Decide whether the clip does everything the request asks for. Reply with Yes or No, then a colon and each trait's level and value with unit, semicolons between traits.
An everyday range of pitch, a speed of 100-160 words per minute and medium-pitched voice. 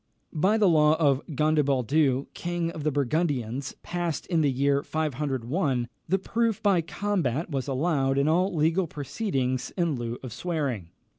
Yes: average, 4.2 semitones; average, 150 wpm; medium, 150 Hz